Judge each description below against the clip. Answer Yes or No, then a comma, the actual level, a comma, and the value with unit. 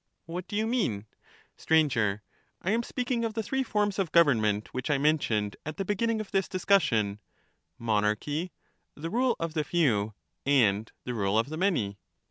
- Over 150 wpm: Yes, average, 175 wpm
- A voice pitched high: No, medium, 155 Hz